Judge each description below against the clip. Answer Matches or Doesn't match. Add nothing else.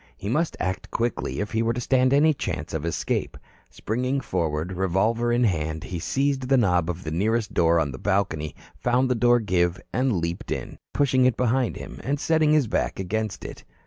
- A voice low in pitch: Matches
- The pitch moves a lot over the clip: Matches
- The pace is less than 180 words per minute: Doesn't match